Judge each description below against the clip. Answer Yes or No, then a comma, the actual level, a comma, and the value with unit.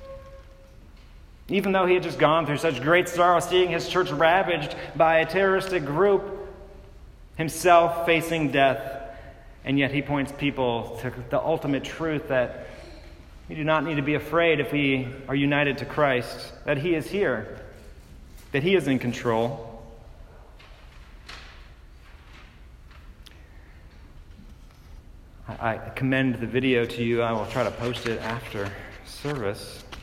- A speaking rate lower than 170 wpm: Yes, slow, 135 wpm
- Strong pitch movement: Yes, wide, 8.0 semitones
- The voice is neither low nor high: No, low, 130 Hz